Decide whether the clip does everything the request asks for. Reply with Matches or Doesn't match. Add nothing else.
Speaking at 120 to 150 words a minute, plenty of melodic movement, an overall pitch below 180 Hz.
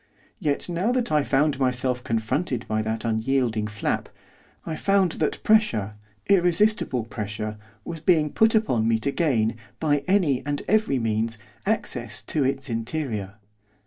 Matches